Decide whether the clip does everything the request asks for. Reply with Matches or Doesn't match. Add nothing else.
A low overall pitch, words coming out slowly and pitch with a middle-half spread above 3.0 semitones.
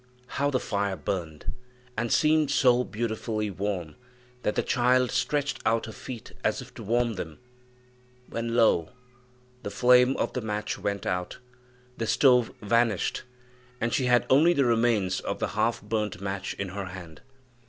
Doesn't match